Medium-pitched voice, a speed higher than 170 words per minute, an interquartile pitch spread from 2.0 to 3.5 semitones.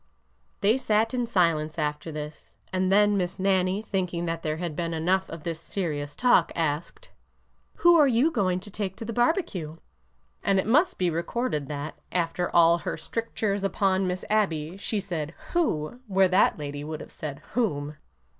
No: medium, 180 Hz; average, 180 wpm; average, 4.7 semitones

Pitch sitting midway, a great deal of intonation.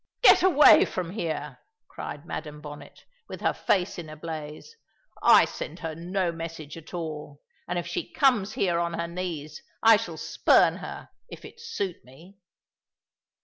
No: medium, 170 Hz; average, 3.6 semitones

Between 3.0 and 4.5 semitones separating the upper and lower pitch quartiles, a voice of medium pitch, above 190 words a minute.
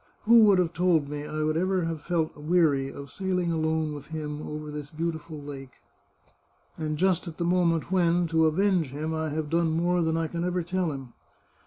No: narrow, 2.6 semitones; medium, 160 Hz; average, 200 wpm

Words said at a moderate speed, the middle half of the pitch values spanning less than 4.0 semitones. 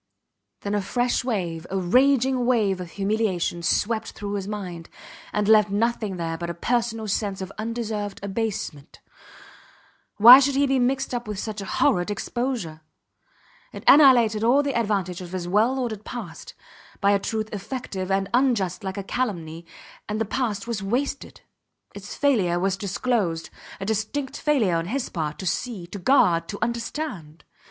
No: average, 160 wpm; average, 4.3 semitones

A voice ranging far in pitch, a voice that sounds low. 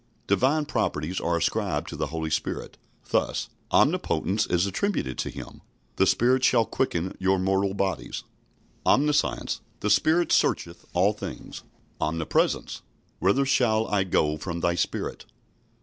Yes: wide, 6.0 semitones; very low, 95 Hz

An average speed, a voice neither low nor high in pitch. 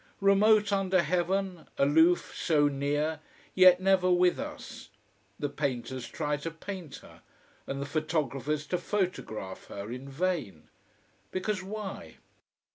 No: slow, 120 wpm; medium, 165 Hz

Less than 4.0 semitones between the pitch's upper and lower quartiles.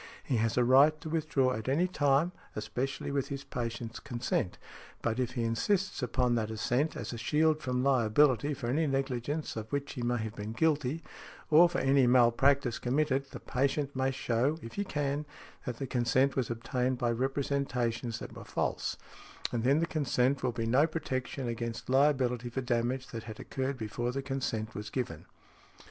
Yes: average, 3.1 semitones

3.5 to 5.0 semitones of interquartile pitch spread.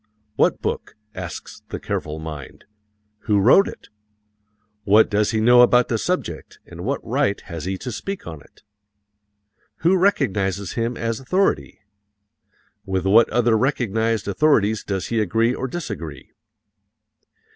Yes: average, 4.4 semitones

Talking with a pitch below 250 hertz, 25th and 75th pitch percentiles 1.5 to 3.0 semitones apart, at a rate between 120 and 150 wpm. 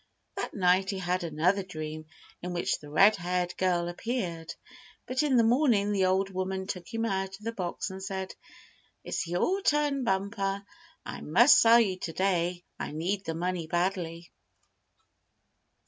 No: high, 190 Hz; narrow, 2.5 semitones; average, 165 wpm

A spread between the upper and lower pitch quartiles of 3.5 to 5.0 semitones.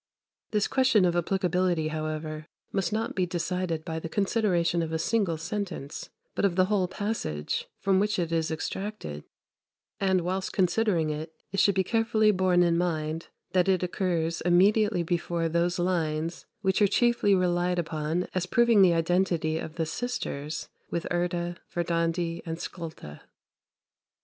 No: average, 2.8 semitones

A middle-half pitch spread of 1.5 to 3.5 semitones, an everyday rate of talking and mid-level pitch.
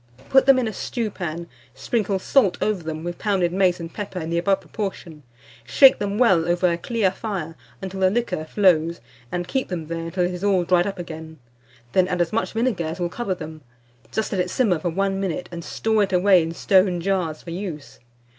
No: average, 3.1 semitones; fast, 210 wpm; medium, 180 Hz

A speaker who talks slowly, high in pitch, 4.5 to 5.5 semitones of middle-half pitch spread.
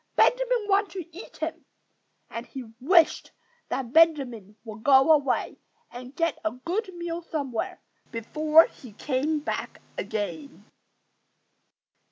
Yes: slow, 120 wpm; very high, 300 Hz; average, 5.0 semitones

